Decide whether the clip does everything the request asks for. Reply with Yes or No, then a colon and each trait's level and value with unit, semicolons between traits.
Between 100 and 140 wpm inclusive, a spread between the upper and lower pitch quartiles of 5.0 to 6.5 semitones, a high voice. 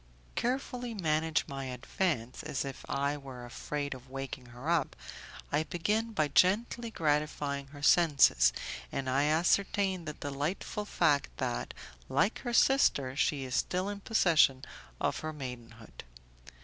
No: slow, 135 wpm; average, 5.3 semitones; medium, 150 Hz